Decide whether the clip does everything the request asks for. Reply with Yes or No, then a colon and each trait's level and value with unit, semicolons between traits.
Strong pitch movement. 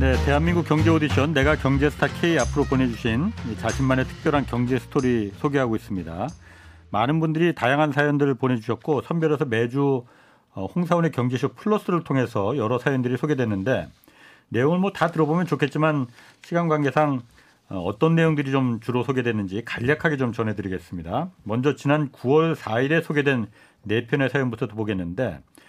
No: average, 4.9 semitones